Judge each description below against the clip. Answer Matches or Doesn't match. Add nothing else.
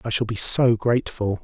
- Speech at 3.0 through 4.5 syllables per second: Doesn't match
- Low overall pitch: Matches